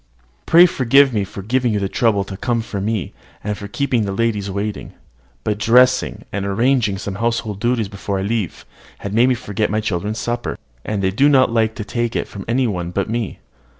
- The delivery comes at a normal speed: No, fast, 210 wpm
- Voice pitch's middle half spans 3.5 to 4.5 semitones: No, average, 3.0 semitones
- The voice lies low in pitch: Yes, low, 110 Hz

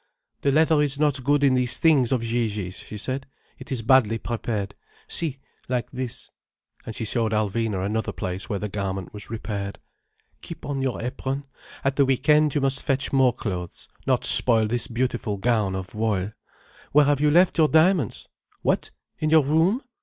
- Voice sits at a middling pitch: No, low, 125 Hz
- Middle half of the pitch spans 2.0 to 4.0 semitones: No, average, 4.8 semitones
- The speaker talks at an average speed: Yes, average, 180 wpm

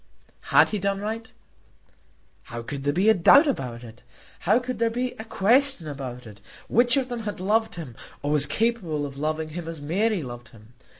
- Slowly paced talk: No, average, 195 wpm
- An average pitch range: No, wide, 8.2 semitones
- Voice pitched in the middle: Yes, medium, 175 Hz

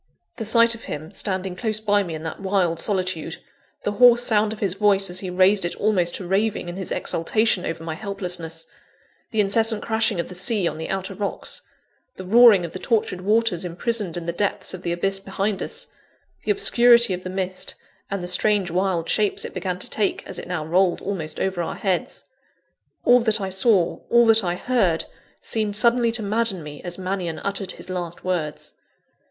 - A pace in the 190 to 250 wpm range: Yes, average, 200 wpm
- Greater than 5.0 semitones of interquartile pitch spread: No, average, 3.5 semitones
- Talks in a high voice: Yes, high, 195 Hz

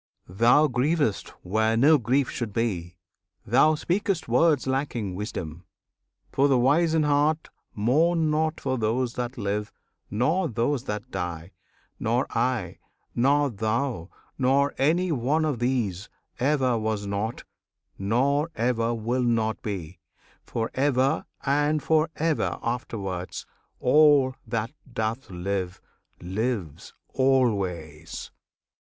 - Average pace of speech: No, slow, 115 wpm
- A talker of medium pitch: No, low, 125 Hz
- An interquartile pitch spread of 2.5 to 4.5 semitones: No, average, 5.2 semitones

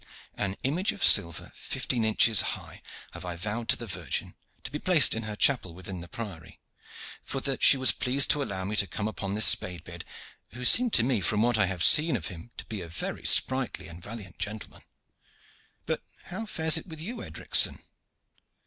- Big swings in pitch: Yes, wide, 6.4 semitones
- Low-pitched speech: Yes, low, 110 Hz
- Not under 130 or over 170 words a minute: No, average, 200 wpm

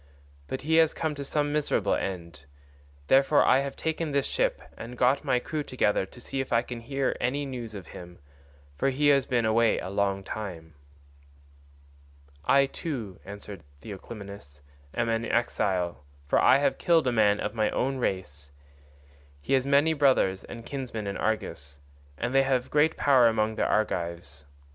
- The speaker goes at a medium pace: Yes, average, 170 wpm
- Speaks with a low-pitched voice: Yes, low, 115 Hz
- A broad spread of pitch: Yes, wide, 5.8 semitones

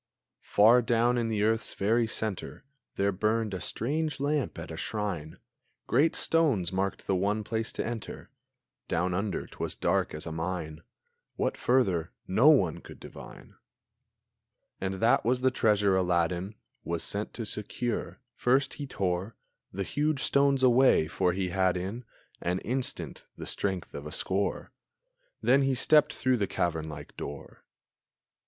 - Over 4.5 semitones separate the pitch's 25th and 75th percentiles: Yes, average, 5.2 semitones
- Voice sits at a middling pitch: No, low, 105 Hz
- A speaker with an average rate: Yes, average, 150 wpm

